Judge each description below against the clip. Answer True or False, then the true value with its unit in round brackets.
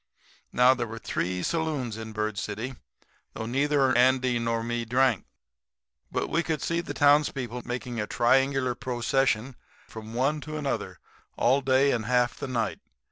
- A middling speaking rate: True (155 wpm)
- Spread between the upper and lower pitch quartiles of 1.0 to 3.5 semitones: True (2.7 semitones)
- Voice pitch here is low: True (125 Hz)